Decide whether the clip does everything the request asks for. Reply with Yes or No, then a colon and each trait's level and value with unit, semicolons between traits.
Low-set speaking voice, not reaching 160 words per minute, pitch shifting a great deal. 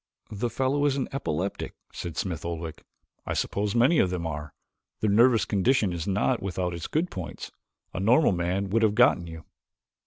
No: low, 100 Hz; average, 180 wpm; wide, 5.8 semitones